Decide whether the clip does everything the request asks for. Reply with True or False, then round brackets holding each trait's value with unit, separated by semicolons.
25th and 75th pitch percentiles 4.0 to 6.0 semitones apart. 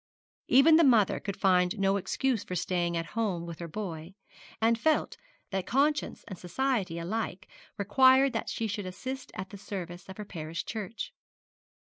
True (4.5 semitones)